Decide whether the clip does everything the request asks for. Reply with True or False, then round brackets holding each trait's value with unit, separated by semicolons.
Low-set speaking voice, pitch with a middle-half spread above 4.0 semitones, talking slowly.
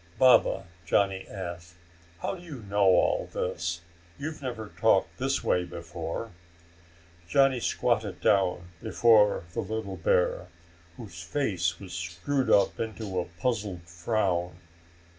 True (95 Hz; 4.4 semitones; 120 wpm)